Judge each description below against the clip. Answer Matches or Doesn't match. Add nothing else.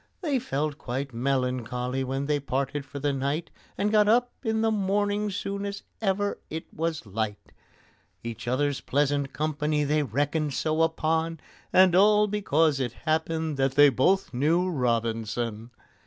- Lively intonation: Matches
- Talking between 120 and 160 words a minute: Matches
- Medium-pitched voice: Matches